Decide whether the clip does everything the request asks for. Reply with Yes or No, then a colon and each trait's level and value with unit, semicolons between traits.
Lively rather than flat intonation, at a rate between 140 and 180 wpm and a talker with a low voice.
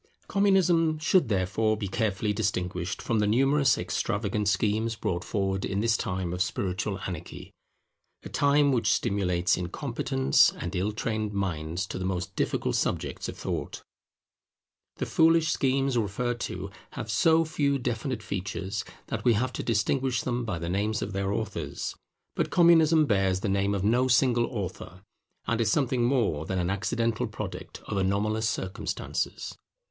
No: average, 4.7 semitones; average, 155 wpm; low, 105 Hz